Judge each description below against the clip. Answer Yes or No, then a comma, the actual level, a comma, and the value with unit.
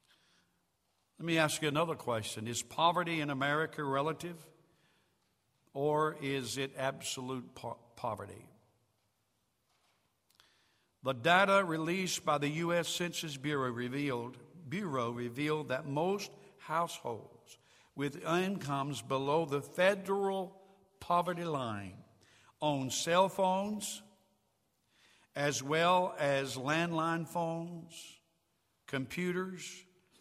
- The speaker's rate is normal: No, slow, 95 wpm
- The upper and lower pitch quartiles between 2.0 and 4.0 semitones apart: No, average, 4.5 semitones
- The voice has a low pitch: No, medium, 155 Hz